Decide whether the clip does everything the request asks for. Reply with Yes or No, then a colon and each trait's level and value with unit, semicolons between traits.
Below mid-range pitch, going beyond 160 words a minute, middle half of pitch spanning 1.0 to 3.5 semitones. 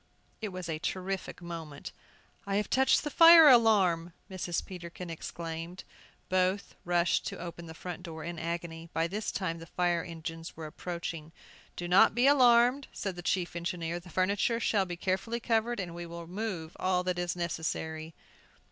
No: medium, 175 Hz; average, 170 wpm; average, 2.9 semitones